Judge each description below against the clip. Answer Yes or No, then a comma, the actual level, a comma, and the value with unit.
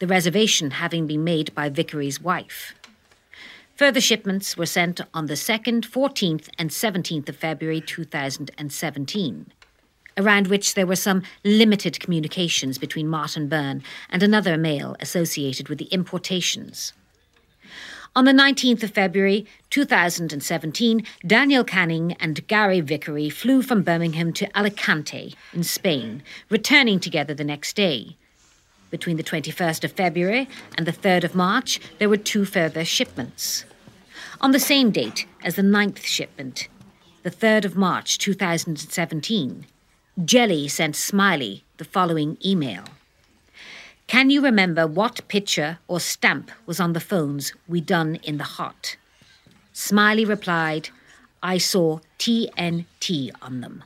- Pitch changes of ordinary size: Yes, average, 4.6 semitones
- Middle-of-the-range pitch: Yes, medium, 175 Hz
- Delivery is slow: Yes, slow, 130 wpm